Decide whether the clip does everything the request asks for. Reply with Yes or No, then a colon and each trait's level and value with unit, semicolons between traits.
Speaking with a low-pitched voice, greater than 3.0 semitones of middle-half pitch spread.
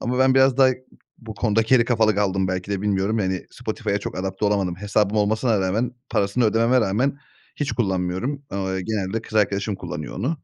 Yes: low, 105 Hz; average, 3.5 semitones